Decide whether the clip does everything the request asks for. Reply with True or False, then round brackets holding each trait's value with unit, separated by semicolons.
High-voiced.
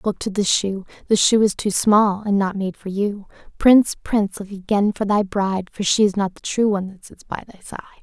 True (200 Hz)